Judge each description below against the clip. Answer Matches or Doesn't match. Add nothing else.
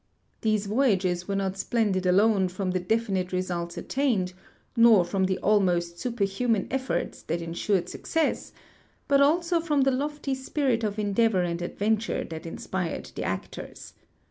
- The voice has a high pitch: Matches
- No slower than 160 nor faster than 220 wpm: Doesn't match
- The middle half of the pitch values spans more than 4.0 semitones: Matches